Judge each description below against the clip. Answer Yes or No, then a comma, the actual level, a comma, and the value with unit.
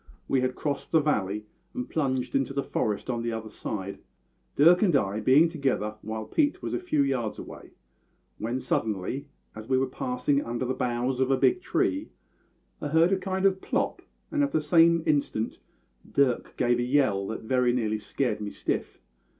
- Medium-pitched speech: No, low, 130 Hz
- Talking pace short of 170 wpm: No, average, 185 wpm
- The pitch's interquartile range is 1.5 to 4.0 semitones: No, wide, 5.4 semitones